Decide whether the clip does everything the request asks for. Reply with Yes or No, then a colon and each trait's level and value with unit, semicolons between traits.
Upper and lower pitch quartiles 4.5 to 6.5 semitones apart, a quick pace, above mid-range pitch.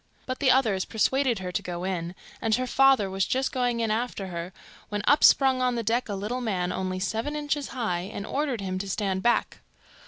Yes: average, 5.1 semitones; fast, 215 wpm; high, 220 Hz